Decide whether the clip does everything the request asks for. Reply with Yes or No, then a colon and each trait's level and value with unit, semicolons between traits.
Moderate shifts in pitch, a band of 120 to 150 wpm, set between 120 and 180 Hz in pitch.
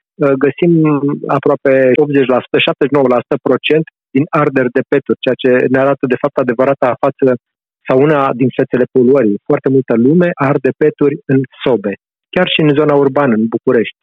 No: narrow, 2.1 semitones; average, 145 wpm; medium, 140 Hz